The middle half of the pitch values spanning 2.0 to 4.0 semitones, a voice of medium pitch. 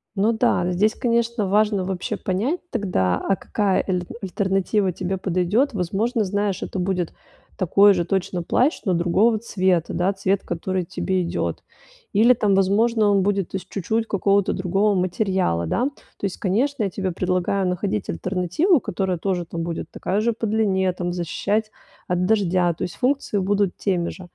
No: average, 2.7 semitones; high, 195 Hz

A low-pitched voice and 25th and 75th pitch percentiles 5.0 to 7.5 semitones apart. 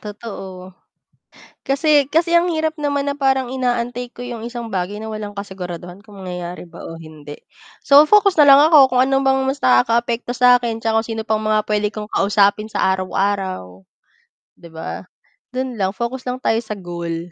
No: high, 225 Hz; wide, 5.5 semitones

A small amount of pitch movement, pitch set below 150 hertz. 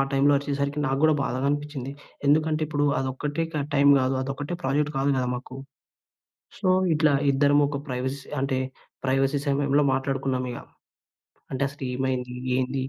Yes: narrow, 1.7 semitones; medium, 140 Hz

